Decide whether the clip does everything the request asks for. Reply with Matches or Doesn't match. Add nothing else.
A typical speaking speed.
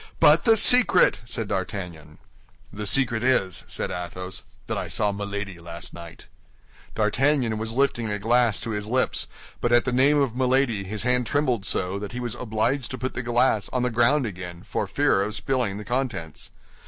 Matches